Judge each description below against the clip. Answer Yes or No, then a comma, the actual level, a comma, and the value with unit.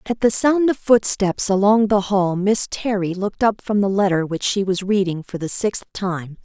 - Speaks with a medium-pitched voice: No, high, 200 Hz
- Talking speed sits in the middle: No, fast, 215 wpm